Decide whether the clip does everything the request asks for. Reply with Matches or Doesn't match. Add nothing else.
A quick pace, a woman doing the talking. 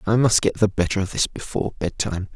Doesn't match